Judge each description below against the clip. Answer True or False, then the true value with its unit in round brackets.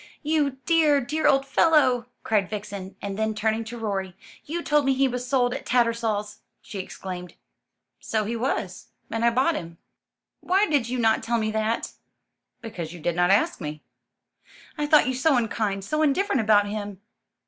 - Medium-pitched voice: False (230 Hz)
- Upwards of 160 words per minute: True (175 wpm)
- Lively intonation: False (4.8 semitones)